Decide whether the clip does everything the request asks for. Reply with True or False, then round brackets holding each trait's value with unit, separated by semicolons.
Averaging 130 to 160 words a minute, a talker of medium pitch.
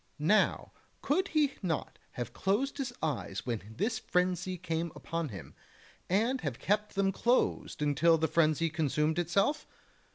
True (140 wpm; 175 Hz)